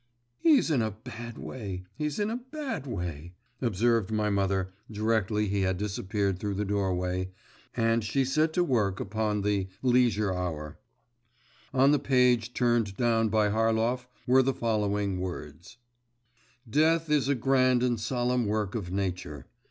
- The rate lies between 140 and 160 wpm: Yes, average, 150 wpm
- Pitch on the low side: Yes, low, 110 Hz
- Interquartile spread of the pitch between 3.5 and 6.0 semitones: Yes, average, 4.3 semitones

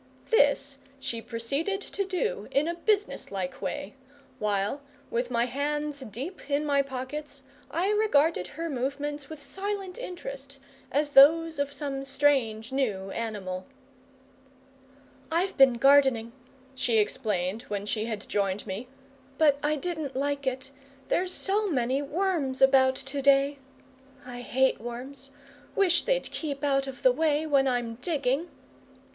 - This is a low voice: No, very high, 275 Hz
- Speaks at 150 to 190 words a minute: No, slow, 135 wpm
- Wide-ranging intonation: No, average, 4.0 semitones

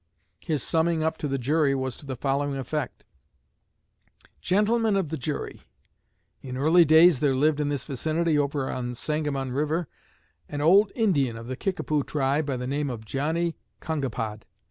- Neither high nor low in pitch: Yes, medium, 145 Hz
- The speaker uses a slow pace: No, average, 165 wpm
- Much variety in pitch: No, average, 3.2 semitones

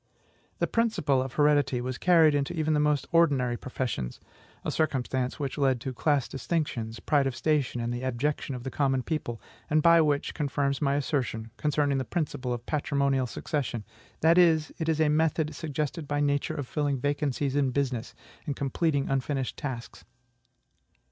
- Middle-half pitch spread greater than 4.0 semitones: No, narrow, 2.6 semitones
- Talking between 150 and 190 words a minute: Yes, average, 160 wpm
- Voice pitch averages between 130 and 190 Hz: Yes, medium, 140 Hz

